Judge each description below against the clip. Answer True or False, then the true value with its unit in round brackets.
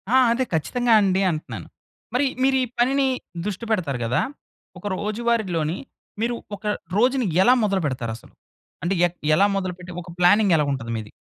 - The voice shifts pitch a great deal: True (6.5 semitones)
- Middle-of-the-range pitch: False (195 Hz)